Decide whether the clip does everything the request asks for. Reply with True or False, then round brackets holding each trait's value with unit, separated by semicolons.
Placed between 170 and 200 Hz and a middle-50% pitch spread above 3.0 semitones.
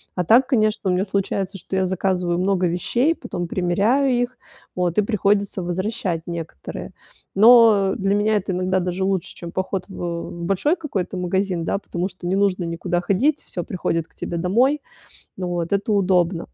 False (190 Hz; 2.7 semitones)